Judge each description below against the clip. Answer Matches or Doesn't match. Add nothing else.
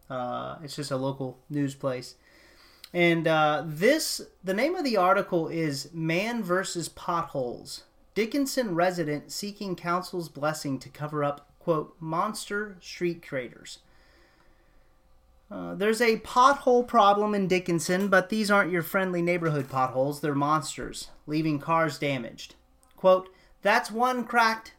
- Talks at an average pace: Doesn't match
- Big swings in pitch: Matches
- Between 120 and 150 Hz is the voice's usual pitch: Doesn't match